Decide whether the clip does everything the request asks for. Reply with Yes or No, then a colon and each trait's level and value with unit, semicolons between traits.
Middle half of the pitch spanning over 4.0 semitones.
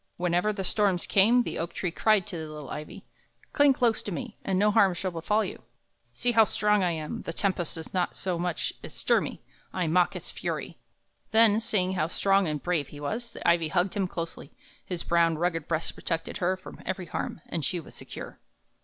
No: average, 3.6 semitones